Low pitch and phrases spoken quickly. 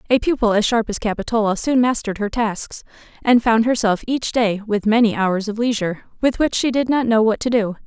No: high, 225 Hz; fast, 220 wpm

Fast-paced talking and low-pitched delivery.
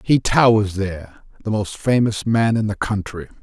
No: average, 175 wpm; low, 105 Hz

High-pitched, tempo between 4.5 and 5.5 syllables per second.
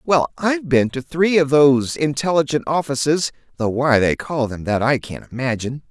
No: medium, 140 Hz; 5.3 syllables/s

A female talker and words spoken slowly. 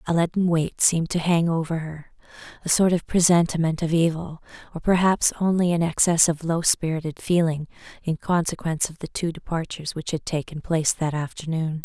No: female; average, 175 wpm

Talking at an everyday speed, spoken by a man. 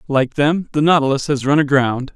Yes: average, 195 wpm; male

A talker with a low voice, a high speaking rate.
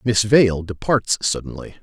No: low, 100 Hz; slow, 130 wpm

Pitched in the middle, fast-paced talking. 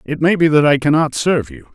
Yes: medium, 145 Hz; fast, 310 wpm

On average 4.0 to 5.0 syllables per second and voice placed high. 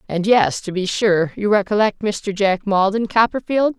Yes: 4.5 syllables/s; high, 205 Hz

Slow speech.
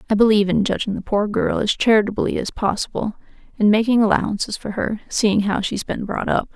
No: average, 200 wpm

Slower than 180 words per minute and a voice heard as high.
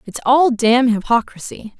Yes: slow, 135 wpm; high, 240 Hz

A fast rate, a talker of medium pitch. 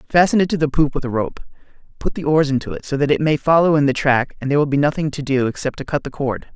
Yes: fast, 300 wpm; medium, 145 Hz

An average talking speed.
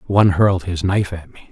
No: fast, 240 wpm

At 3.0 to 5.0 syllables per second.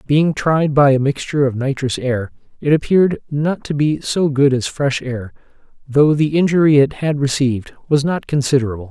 No: 5.2 syllables/s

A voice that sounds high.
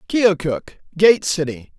No: medium, 175 Hz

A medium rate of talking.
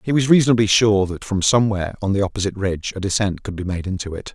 No: fast, 250 wpm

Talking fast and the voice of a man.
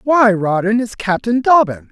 No: average, 155 wpm; male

